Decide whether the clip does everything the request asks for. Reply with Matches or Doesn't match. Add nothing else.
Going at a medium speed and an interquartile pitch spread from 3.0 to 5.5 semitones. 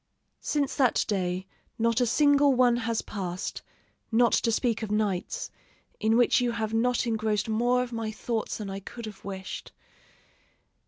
Doesn't match